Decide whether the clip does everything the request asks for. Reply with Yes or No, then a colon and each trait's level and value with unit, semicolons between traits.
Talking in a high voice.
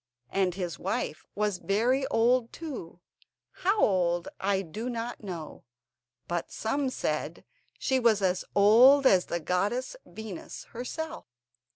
Yes: high, 215 Hz